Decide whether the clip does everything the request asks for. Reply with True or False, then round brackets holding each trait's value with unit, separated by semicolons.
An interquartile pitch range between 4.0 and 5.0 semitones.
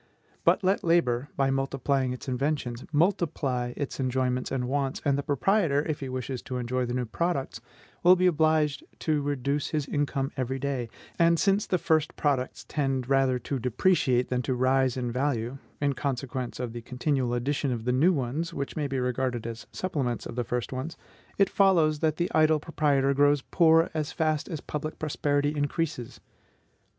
False (3.5 semitones)